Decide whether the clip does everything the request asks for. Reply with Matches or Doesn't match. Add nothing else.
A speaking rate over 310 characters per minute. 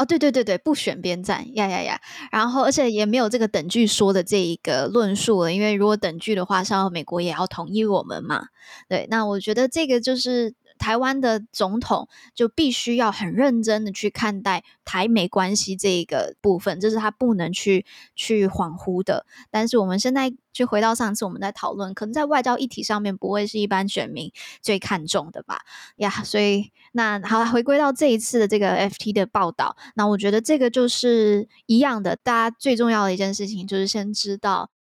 Matches